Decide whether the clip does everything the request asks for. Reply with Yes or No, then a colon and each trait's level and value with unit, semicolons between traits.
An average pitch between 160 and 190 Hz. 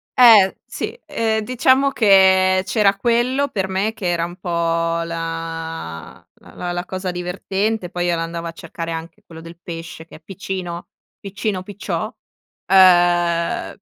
Yes: medium, 185 Hz